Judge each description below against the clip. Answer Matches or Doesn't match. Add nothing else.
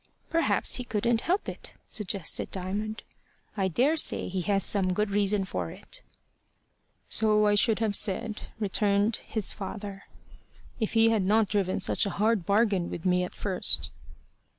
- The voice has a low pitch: Doesn't match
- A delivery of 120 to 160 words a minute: Matches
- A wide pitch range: Doesn't match